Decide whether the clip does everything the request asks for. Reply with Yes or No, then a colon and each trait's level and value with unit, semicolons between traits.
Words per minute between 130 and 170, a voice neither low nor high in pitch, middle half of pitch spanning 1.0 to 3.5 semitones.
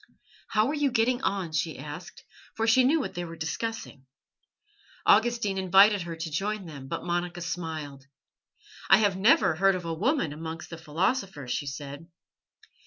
No: average, 165 wpm; medium, 175 Hz; average, 5.1 semitones